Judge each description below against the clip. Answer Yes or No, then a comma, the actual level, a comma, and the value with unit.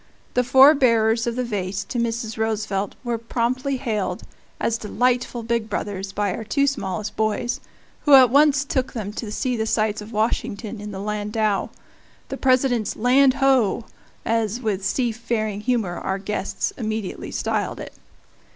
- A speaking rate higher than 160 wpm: No, average, 155 wpm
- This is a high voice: Yes, high, 225 Hz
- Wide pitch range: No, average, 2.9 semitones